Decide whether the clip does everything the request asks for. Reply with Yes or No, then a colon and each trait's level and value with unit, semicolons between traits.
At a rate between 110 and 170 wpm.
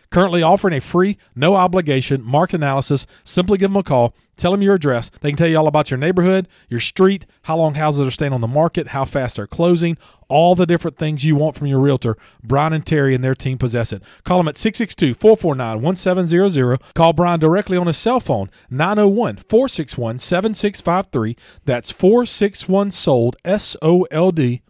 No: average, 180 wpm